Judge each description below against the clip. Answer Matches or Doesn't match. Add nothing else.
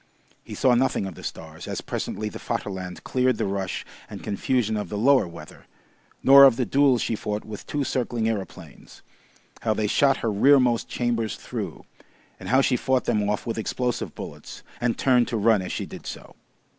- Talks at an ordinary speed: Matches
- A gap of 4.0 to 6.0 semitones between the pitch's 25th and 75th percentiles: Doesn't match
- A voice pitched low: Matches